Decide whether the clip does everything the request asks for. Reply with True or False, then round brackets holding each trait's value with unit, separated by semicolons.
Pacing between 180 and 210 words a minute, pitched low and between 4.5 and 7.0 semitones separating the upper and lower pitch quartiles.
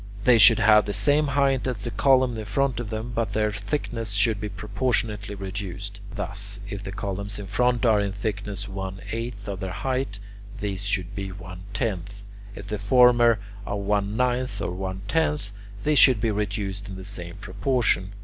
False (185 wpm; 105 Hz; 3.0 semitones)